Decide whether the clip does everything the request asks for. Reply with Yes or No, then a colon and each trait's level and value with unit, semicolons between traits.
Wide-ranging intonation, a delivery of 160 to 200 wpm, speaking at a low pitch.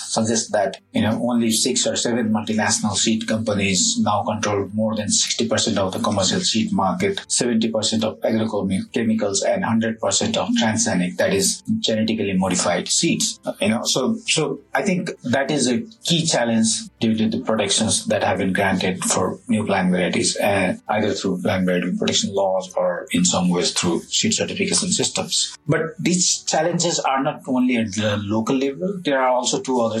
Yes: wide, 7.3 semitones; average, 170 wpm; low, 115 Hz